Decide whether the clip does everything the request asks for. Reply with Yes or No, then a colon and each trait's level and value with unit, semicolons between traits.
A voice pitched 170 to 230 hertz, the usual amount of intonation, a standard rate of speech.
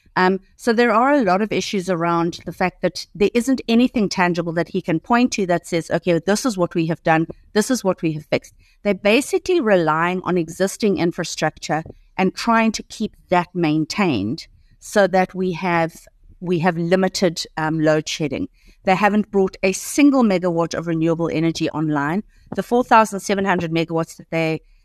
Yes: medium, 185 Hz; average, 3.5 semitones; average, 180 wpm